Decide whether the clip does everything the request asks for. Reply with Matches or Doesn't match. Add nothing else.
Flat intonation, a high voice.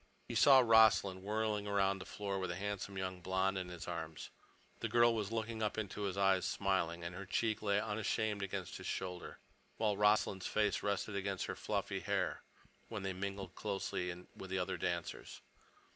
Doesn't match